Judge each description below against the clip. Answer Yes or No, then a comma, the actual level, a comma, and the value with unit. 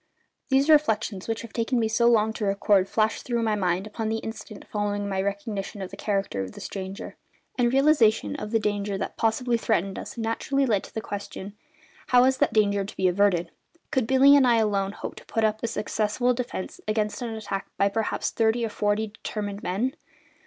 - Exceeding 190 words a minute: Yes, fast, 205 wpm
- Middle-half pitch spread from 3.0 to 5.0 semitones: No, narrow, 2.6 semitones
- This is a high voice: Yes, high, 215 Hz